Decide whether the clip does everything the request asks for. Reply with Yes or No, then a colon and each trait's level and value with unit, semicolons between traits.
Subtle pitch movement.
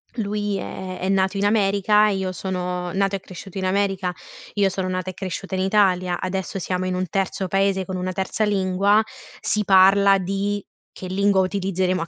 Yes: narrow, 1.3 semitones